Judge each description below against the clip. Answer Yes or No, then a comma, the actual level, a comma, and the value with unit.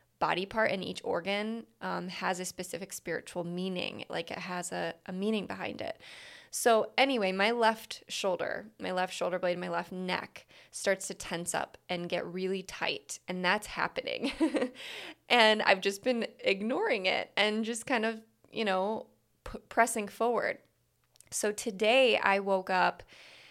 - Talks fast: No, average, 160 wpm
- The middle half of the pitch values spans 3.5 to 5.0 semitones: Yes, average, 3.9 semitones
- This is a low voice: No, high, 205 Hz